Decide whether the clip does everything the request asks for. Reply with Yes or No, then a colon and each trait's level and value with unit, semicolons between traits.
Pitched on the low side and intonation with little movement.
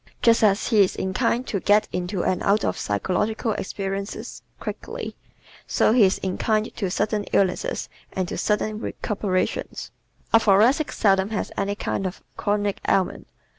No: high, 205 Hz; narrow, 2.2 semitones